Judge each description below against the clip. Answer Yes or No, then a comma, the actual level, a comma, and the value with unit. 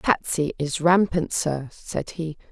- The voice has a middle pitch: Yes, medium, 160 Hz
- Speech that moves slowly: No, average, 145 wpm